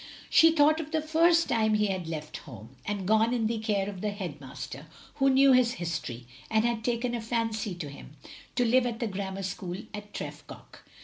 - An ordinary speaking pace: No, fast, 210 wpm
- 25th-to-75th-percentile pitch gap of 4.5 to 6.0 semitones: Yes, average, 5.1 semitones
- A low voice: No, high, 220 Hz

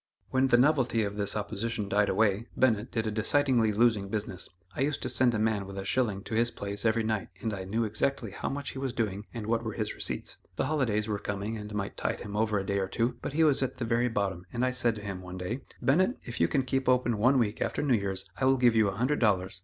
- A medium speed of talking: No, fast, 265 wpm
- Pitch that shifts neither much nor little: Yes, average, 3.7 semitones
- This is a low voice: Yes, low, 110 Hz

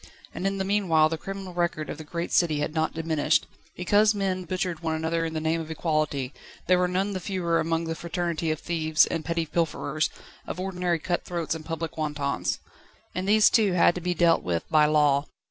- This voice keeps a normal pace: No, fast, 210 wpm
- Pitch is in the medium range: Yes, medium, 165 Hz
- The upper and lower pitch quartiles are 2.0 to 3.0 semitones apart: Yes, narrow, 2.5 semitones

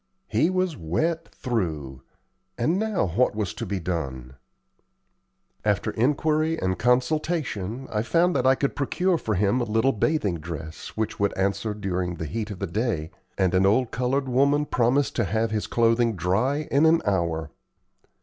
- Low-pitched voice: Yes, low, 110 Hz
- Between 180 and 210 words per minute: No, average, 165 wpm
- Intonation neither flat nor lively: No, wide, 7.1 semitones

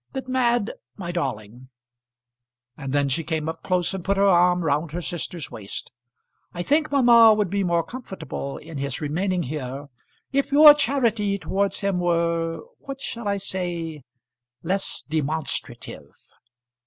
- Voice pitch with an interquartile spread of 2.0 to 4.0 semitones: No, average, 4.8 semitones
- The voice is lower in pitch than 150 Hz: No, medium, 175 Hz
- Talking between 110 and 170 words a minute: Yes, average, 145 wpm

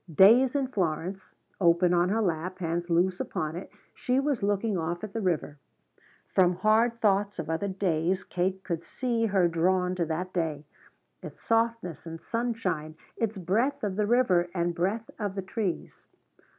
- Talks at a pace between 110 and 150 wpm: No, average, 165 wpm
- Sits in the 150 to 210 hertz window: Yes, medium, 185 Hz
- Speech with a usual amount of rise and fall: Yes, average, 4.2 semitones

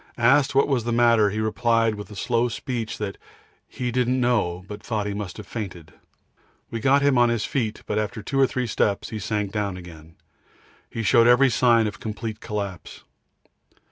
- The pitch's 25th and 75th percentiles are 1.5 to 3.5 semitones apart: Yes, average, 2.8 semitones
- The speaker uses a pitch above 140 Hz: No, low, 110 Hz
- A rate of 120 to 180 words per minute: No, average, 190 wpm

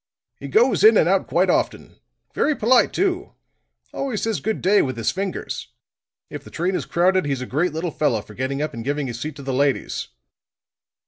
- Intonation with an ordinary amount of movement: No, wide, 7.3 semitones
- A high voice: No, medium, 155 Hz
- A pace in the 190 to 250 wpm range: Yes, average, 200 wpm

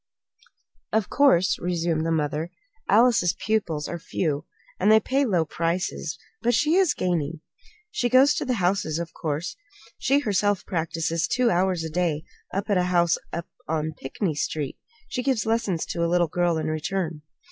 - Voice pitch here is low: No, medium, 175 Hz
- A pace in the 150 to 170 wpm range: Yes, average, 165 wpm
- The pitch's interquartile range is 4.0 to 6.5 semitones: Yes, average, 4.9 semitones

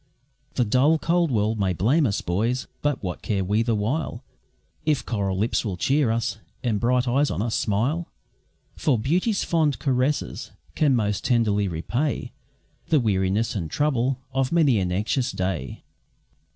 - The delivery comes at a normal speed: Yes, average, 155 wpm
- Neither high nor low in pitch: No, low, 120 Hz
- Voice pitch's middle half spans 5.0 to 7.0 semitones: Yes, wide, 5.5 semitones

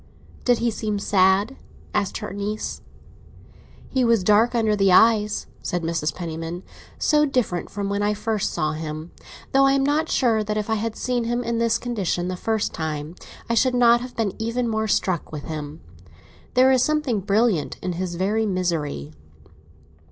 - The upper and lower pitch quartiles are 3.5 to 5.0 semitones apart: Yes, average, 4.6 semitones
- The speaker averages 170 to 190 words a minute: Yes, average, 175 wpm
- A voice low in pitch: No, high, 210 Hz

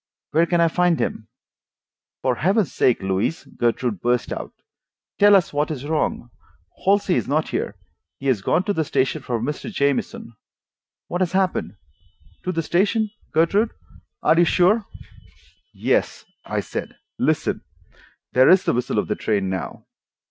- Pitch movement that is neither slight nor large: No, wide, 7.0 semitones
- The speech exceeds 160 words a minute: No, average, 155 wpm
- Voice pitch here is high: No, medium, 160 Hz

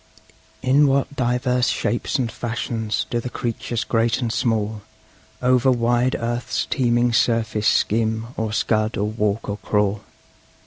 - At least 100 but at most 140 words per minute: Yes, slow, 135 wpm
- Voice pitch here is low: Yes, low, 115 Hz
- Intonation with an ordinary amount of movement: No, narrow, 2.0 semitones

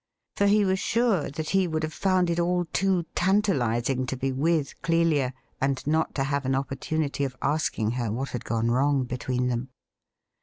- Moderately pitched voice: Yes, medium, 145 Hz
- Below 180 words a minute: No, average, 185 wpm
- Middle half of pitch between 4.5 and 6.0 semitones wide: Yes, average, 5.1 semitones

